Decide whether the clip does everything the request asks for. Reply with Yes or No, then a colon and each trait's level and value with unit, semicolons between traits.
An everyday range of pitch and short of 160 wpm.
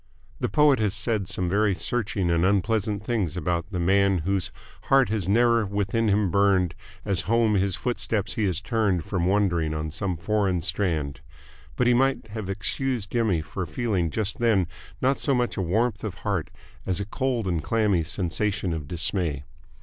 No: average, 3.7 semitones; average, 175 wpm